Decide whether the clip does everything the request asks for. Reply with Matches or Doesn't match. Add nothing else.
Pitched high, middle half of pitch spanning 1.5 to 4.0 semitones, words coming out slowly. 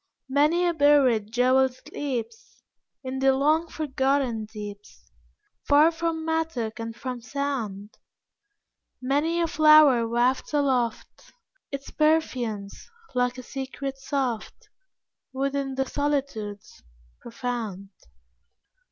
Matches